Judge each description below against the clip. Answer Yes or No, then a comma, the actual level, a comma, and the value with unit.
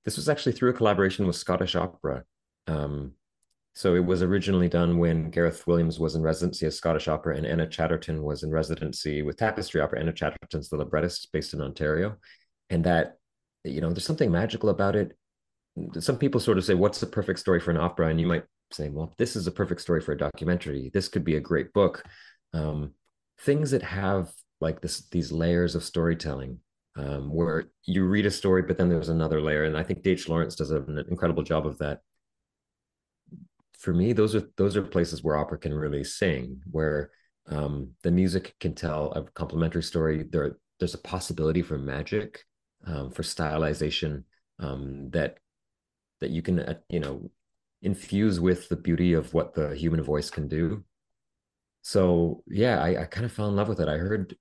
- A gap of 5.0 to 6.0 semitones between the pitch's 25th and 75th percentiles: No, average, 3.0 semitones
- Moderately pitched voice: No, very low, 85 Hz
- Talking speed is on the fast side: No, average, 190 wpm